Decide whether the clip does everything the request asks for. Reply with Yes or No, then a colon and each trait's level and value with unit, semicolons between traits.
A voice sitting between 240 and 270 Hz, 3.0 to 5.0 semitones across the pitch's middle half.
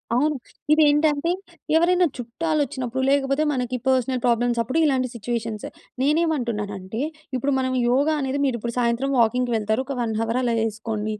Yes: very high, 250 Hz; average, 3.6 semitones